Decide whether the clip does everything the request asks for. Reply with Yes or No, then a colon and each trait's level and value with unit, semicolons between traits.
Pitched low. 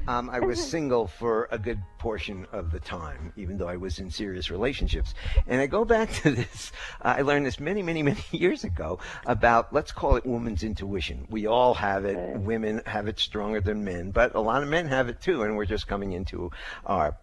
Yes: low, 105 Hz